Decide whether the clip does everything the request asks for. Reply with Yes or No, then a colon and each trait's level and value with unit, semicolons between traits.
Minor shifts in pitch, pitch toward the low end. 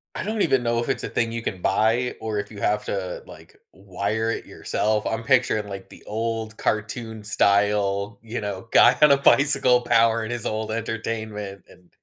Yes: narrow, 2.1 semitones; low, 110 Hz